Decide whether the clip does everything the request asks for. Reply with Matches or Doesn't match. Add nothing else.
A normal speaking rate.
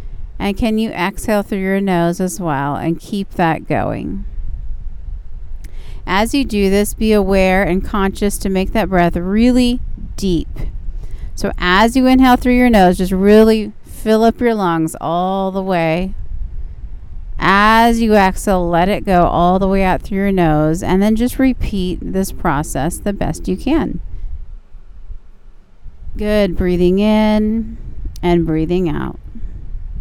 Matches